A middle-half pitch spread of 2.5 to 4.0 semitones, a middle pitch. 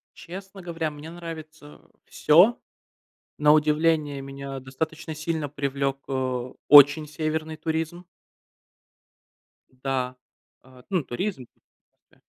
Yes: average, 2.9 semitones; medium, 150 Hz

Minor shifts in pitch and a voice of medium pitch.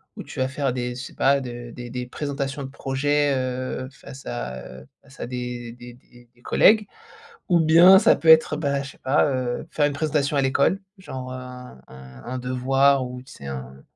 No: narrow, 2.3 semitones; low, 130 Hz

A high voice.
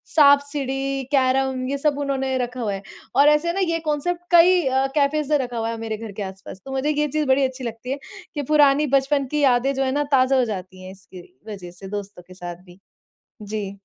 Yes: very high, 265 Hz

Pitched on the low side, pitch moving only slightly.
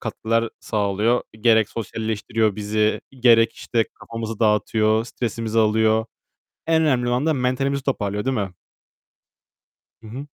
Yes: low, 115 Hz; narrow, 2.3 semitones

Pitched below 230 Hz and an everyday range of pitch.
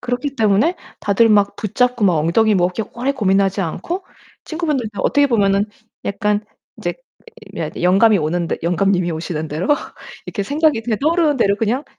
Yes: high, 210 Hz; average, 4.7 semitones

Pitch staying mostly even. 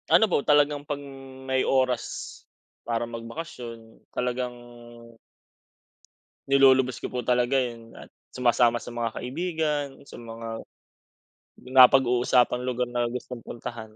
Yes: narrow, 2.1 semitones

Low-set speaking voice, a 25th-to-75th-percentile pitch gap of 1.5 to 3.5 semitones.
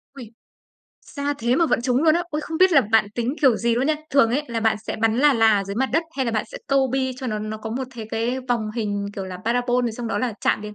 No: high, 240 Hz; average, 3.2 semitones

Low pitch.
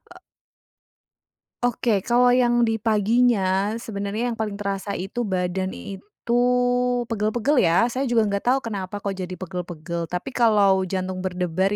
No: high, 205 Hz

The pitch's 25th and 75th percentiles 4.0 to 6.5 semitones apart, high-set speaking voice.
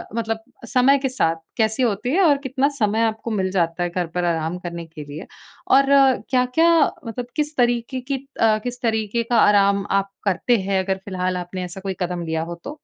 Yes: wide, 5.5 semitones; high, 210 Hz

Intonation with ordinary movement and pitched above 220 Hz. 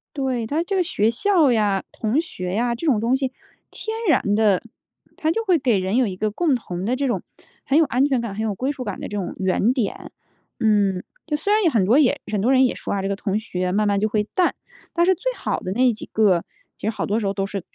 No: wide, 5.9 semitones; high, 230 Hz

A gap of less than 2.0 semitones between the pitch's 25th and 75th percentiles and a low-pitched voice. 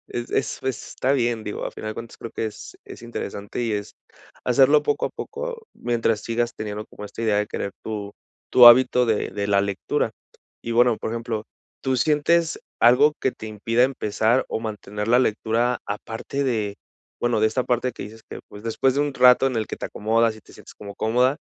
No: average, 2.9 semitones; low, 115 Hz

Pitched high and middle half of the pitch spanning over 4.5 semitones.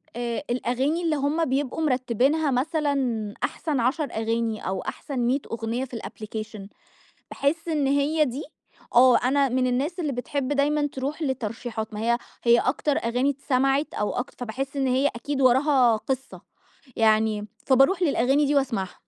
No: very high, 260 Hz; average, 3.3 semitones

